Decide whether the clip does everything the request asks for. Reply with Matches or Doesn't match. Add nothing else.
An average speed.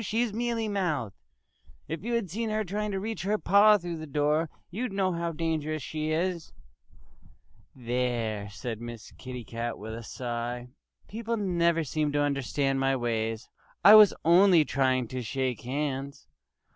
Matches